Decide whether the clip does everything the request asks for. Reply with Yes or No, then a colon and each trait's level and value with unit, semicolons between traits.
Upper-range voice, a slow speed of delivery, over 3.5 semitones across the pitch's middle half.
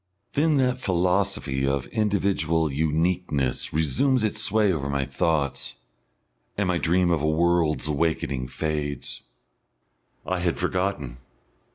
No: very low, 85 Hz; slow, 120 wpm; average, 4.4 semitones